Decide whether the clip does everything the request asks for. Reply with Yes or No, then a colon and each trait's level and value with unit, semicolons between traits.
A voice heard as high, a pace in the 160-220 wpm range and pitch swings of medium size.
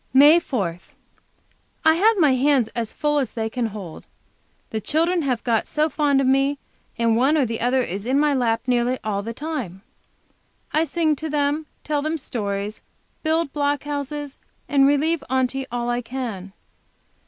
Yes: very high, 270 Hz; average, 170 wpm; average, 4.3 semitones